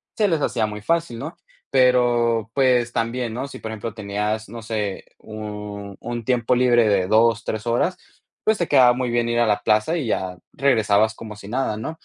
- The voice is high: No, low, 115 Hz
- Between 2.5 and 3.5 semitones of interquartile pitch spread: Yes, average, 2.8 semitones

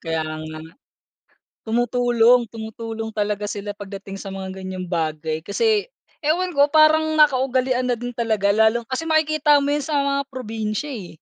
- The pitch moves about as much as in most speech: No, wide, 5.8 semitones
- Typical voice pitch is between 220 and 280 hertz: Yes, high, 230 Hz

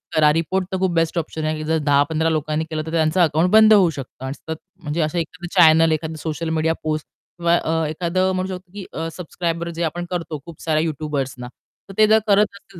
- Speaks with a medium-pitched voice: Yes, medium, 165 Hz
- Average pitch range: No, narrow, 2.2 semitones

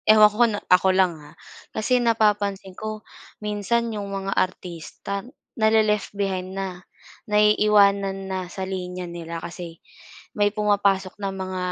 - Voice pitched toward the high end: Yes, high, 195 Hz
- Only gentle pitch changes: Yes, narrow, 2.1 semitones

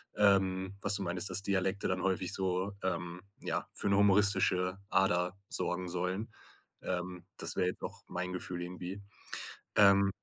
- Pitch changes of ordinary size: No, narrow, 1.5 semitones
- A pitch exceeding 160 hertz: No, very low, 95 Hz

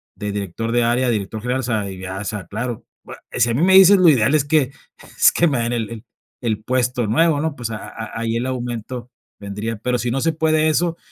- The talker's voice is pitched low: Yes, low, 120 Hz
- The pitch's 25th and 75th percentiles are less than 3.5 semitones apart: No, average, 4.4 semitones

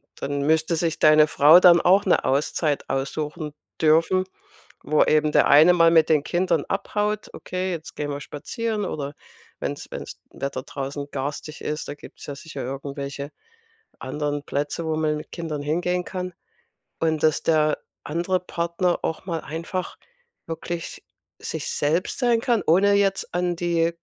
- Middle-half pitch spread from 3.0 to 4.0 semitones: Yes, average, 3.3 semitones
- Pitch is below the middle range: No, medium, 160 Hz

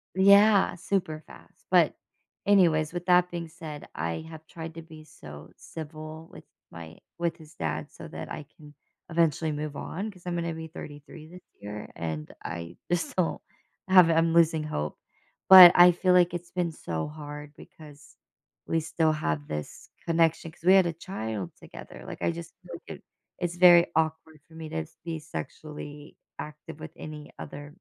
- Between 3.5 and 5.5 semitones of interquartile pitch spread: No, narrow, 2.6 semitones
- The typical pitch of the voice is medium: Yes, medium, 160 Hz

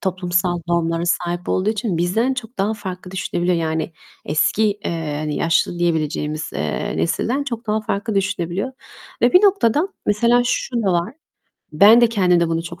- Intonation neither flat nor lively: Yes, average, 4.8 semitones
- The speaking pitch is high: No, medium, 180 Hz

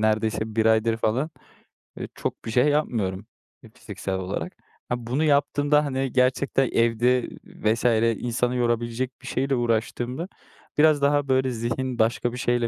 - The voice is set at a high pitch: No, low, 120 Hz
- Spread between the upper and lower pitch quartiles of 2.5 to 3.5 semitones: Yes, average, 2.9 semitones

